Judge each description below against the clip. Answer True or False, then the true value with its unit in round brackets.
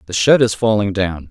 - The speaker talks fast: True (230 wpm)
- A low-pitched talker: True (105 Hz)